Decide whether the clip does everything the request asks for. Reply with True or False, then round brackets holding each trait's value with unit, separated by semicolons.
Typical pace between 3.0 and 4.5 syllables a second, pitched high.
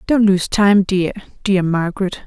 True (4.4 syllables/s; 195 Hz)